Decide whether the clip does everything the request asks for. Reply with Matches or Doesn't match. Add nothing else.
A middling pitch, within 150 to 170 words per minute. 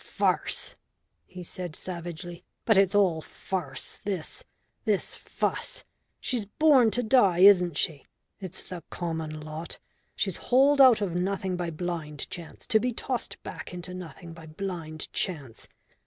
Doesn't match